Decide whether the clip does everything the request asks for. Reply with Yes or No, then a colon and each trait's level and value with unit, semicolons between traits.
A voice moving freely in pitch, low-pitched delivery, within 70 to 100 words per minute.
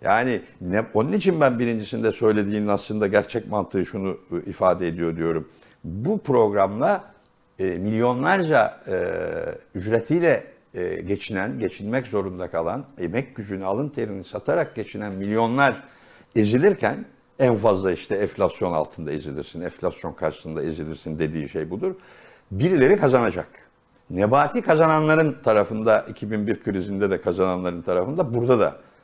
No: wide, 6.9 semitones; low, 110 Hz; average, 120 wpm